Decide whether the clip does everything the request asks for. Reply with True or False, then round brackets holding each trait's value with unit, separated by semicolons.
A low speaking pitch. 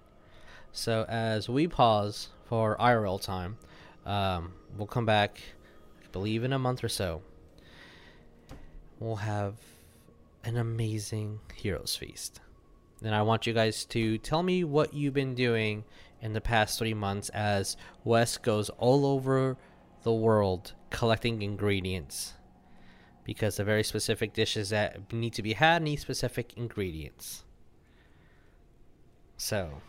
True (110 Hz)